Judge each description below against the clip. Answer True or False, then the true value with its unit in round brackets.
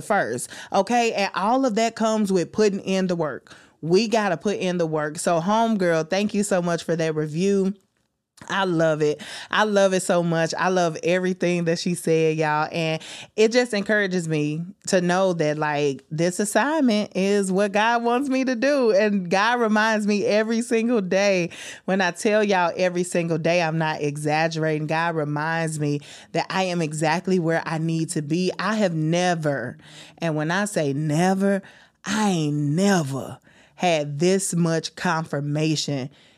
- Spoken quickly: False (175 wpm)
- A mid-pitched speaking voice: True (175 Hz)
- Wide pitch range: False (4.2 semitones)